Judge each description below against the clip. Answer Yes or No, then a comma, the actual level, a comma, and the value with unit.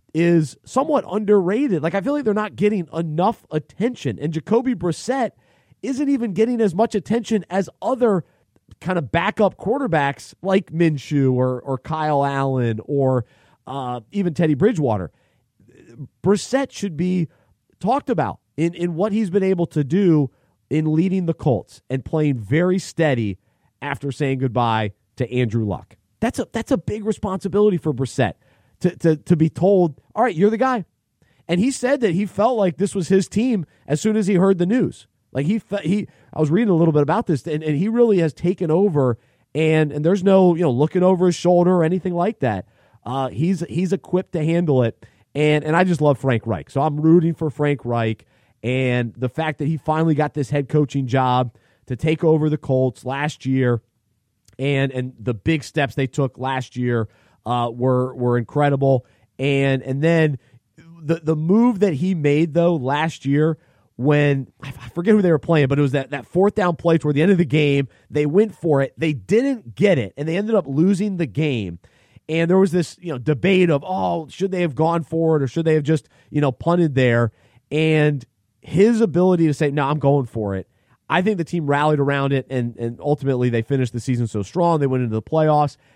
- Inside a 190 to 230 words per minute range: Yes, average, 200 wpm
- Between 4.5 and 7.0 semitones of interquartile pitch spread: Yes, wide, 5.5 semitones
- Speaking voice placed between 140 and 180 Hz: Yes, medium, 155 Hz